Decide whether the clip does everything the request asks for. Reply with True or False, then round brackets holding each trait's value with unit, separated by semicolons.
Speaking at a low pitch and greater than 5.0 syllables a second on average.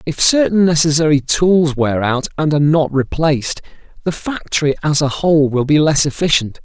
False (150 Hz; 5.3 syllables/s)